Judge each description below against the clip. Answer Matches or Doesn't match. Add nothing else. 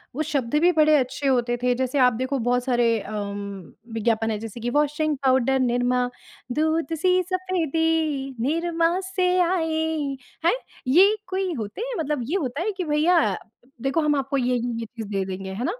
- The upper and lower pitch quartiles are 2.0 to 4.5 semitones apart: Doesn't match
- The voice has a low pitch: Doesn't match